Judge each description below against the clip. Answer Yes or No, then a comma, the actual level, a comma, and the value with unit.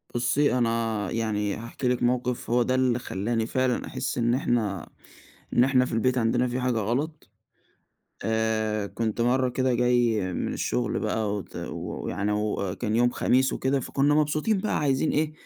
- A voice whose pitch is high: No, low, 120 Hz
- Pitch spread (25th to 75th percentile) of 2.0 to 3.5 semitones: Yes, narrow, 2.6 semitones